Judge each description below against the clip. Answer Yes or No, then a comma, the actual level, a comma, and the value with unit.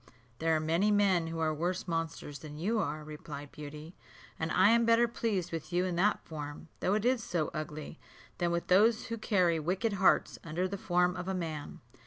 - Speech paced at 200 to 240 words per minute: Yes, fast, 205 wpm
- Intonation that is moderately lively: Yes, average, 4.0 semitones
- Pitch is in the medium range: Yes, medium, 175 Hz